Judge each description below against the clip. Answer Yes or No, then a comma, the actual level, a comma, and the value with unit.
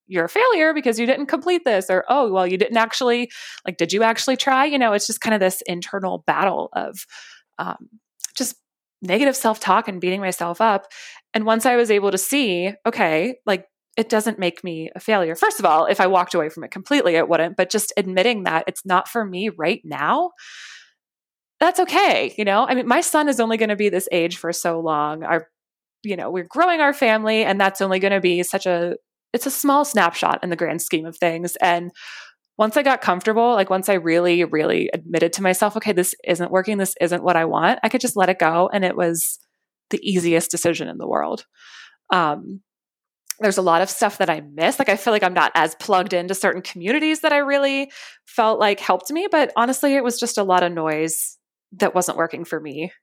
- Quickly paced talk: Yes, fast, 220 wpm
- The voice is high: Yes, high, 200 Hz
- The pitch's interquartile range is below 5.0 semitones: No, average, 5.3 semitones